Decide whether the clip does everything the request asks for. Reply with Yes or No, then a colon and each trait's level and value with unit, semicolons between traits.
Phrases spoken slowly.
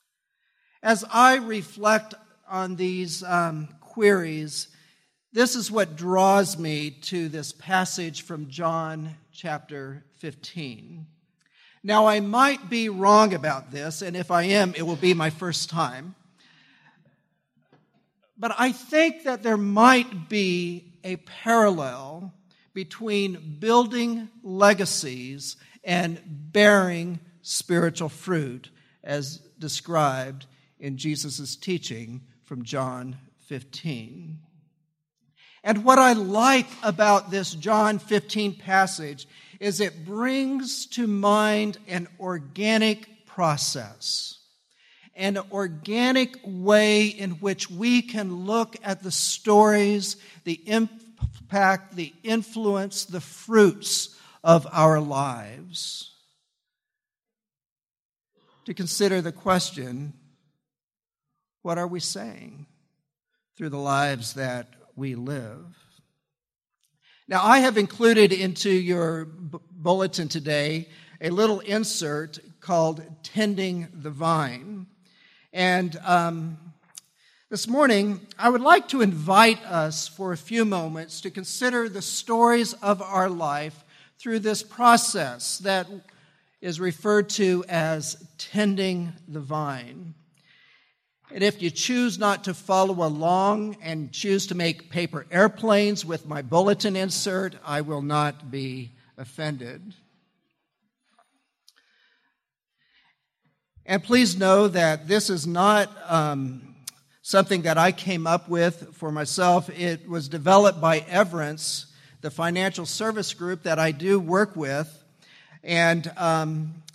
Yes: slow, 110 wpm